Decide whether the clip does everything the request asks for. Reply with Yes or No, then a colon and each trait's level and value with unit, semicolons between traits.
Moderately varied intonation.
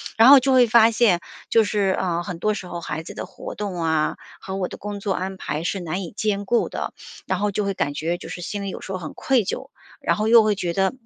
Yes: average, 3.3 semitones